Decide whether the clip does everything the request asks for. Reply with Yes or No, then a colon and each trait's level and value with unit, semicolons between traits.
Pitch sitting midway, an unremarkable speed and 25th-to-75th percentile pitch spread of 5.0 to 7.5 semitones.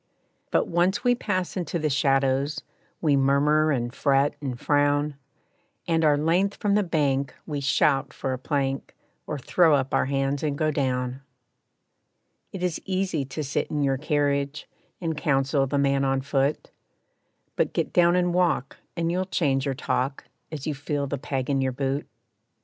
No: medium, 145 Hz; average, 170 wpm; average, 2.8 semitones